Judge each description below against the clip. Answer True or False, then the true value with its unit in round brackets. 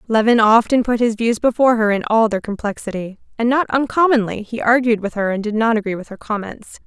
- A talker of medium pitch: False (225 Hz)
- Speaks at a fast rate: True (220 wpm)